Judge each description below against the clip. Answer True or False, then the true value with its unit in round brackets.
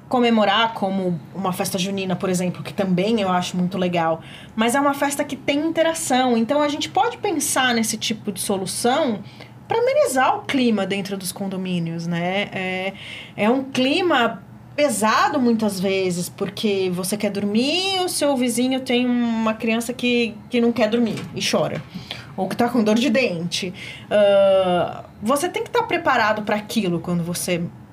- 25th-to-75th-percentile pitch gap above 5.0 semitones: True (5.6 semitones)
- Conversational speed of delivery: True (170 wpm)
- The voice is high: True (215 Hz)